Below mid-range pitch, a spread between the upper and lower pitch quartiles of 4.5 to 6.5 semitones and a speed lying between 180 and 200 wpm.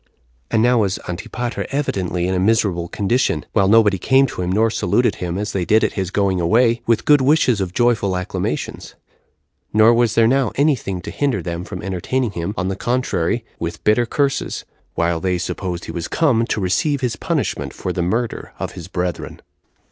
Yes: low, 105 Hz; average, 4.9 semitones; average, 195 wpm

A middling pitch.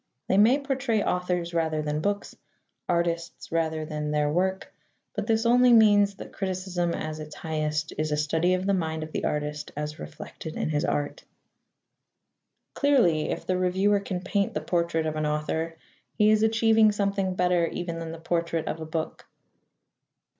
Yes: medium, 170 Hz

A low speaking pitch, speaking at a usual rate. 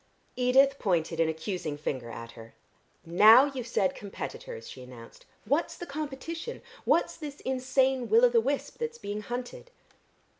No: very high, 250 Hz; average, 150 wpm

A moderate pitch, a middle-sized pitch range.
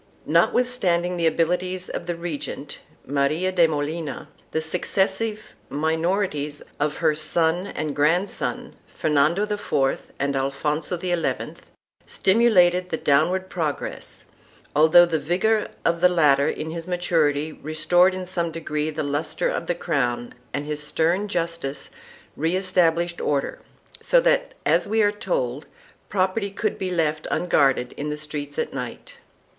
Yes: medium, 165 Hz; average, 3.4 semitones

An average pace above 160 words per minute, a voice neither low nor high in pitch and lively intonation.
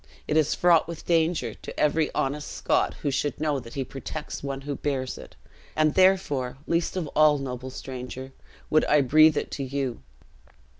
No: average, 180 wpm; medium, 145 Hz; average, 2.7 semitones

